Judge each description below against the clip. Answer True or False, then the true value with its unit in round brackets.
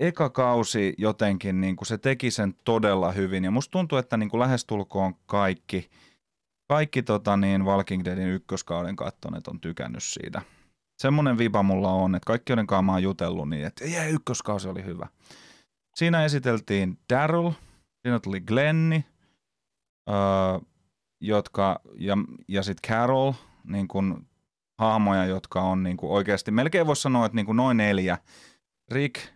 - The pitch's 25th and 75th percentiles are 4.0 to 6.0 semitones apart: True (4.7 semitones)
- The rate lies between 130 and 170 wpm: True (145 wpm)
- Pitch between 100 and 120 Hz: True (105 Hz)